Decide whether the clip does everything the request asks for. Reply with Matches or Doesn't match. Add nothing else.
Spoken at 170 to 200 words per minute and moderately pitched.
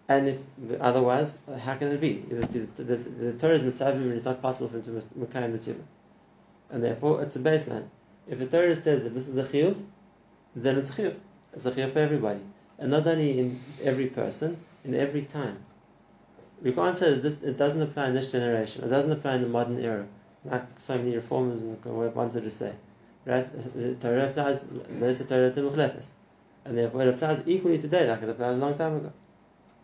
Doesn't match